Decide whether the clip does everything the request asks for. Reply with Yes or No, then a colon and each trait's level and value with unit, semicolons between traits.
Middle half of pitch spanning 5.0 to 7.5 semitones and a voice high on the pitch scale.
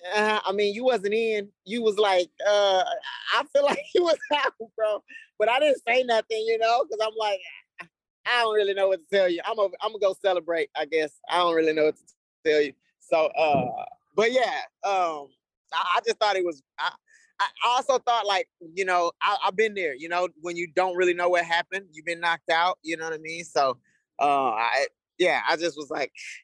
Yes: wide, 5.4 semitones; high, 205 Hz